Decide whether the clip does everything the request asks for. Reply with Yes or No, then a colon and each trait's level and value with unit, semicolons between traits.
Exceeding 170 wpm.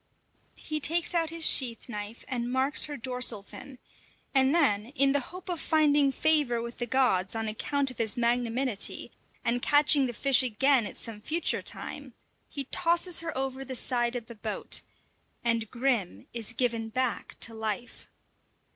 No: average, 165 wpm